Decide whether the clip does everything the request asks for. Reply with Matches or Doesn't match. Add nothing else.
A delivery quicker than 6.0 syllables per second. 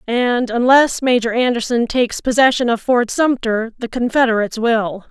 Doesn't match